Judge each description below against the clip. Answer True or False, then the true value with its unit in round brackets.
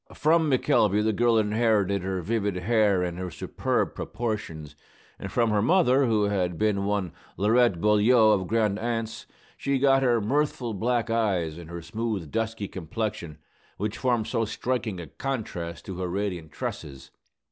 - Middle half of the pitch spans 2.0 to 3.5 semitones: False (3.9 semitones)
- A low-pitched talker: True (105 Hz)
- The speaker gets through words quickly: False (160 wpm)